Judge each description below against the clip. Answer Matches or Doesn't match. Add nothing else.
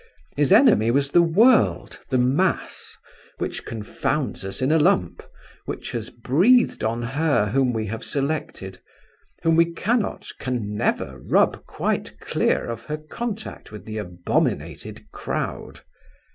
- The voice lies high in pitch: Doesn't match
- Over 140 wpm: Doesn't match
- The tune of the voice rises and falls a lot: Matches